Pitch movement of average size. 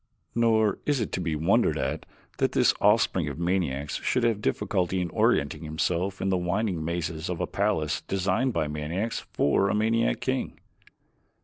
Yes: average, 4.5 semitones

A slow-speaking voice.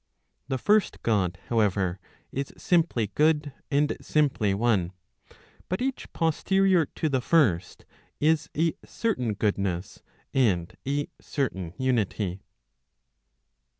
Yes: slow, 105 wpm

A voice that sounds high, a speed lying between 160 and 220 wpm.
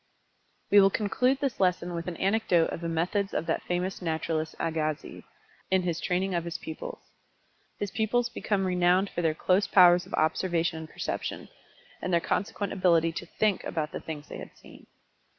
No: medium, 180 Hz; average, 180 wpm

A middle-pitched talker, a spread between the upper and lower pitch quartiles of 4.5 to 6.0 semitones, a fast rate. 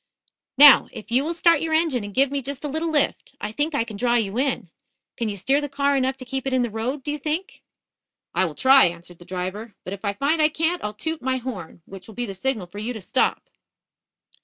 No: very high, 260 Hz; wide, 5.6 semitones; fast, 255 wpm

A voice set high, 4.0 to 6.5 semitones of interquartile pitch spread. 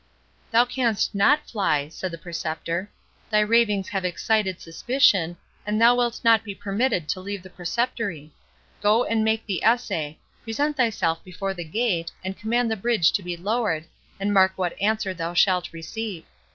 Yes: high, 200 Hz; average, 4.5 semitones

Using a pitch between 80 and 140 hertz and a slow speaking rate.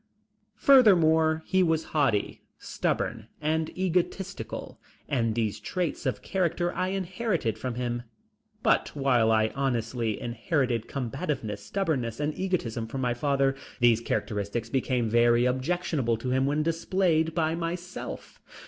Yes: low, 135 Hz; slow, 125 wpm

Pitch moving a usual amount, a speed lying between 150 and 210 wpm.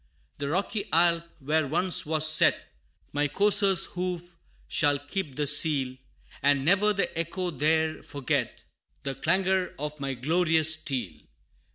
No: average, 3.8 semitones; slow, 135 wpm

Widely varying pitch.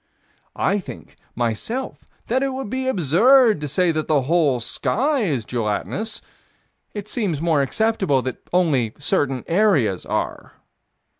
Yes: wide, 8.7 semitones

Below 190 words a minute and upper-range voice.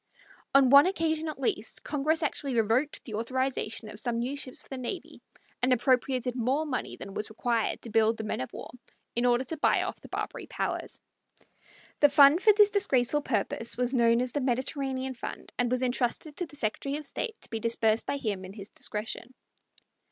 No: average, 195 wpm; very high, 255 Hz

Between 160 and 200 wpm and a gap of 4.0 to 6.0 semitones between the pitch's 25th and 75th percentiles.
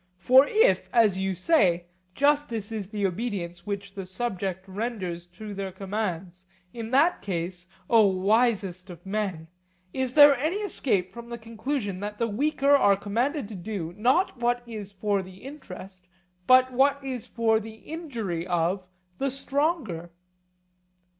No: average, 145 wpm; average, 5.3 semitones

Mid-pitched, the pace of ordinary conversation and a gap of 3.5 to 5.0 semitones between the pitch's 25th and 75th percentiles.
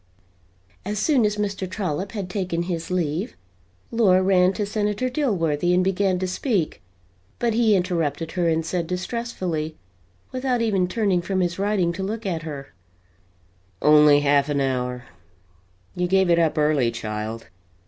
Yes: medium, 180 Hz; average, 150 wpm; average, 4.4 semitones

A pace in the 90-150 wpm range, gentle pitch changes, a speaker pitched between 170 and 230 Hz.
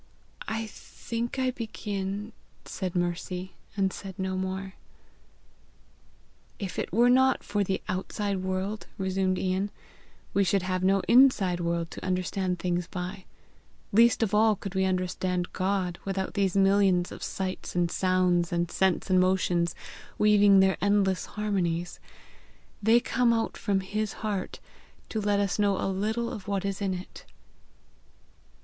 Yes: average, 145 wpm; narrow, 1.9 semitones; high, 190 Hz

